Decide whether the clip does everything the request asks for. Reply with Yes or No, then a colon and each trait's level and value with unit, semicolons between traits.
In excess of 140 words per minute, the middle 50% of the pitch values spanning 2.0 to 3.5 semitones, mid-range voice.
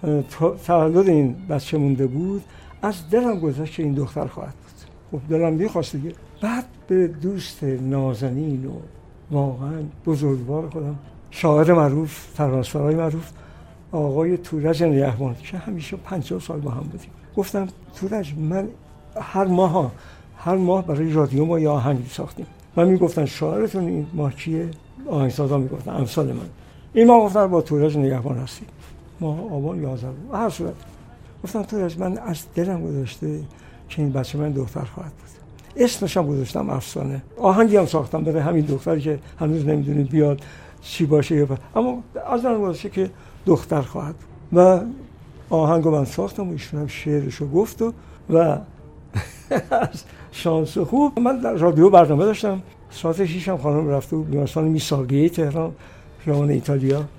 No: average, 150 wpm; average, 4.1 semitones; medium, 155 Hz